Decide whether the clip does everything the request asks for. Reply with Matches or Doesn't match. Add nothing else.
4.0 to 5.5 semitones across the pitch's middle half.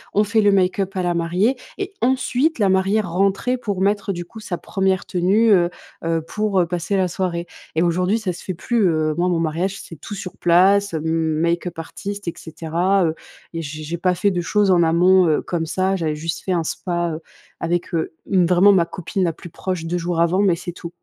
Doesn't match